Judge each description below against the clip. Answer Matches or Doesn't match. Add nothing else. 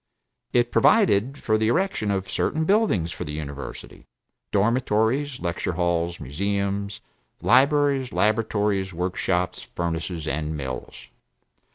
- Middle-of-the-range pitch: Doesn't match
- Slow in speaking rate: Matches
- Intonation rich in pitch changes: Matches